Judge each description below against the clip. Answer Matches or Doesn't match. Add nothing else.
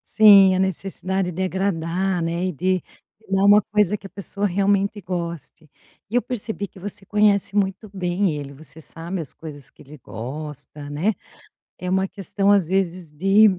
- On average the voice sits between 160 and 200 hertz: Matches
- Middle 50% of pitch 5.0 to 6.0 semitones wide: Doesn't match